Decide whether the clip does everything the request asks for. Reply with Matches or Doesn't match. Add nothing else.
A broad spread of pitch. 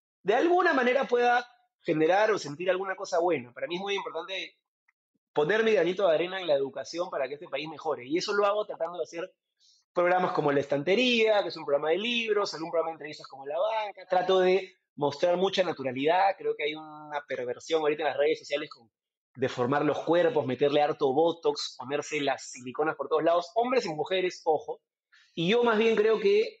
Matches